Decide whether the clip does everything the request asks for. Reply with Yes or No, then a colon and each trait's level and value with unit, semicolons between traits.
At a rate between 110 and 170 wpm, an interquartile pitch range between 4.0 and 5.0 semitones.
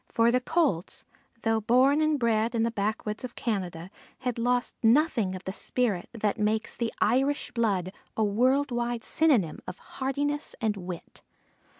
No: average, 160 wpm; average, 3.4 semitones